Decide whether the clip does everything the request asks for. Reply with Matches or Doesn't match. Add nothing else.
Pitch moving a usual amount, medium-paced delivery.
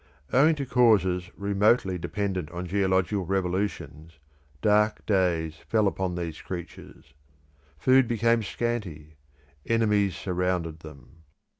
Doesn't match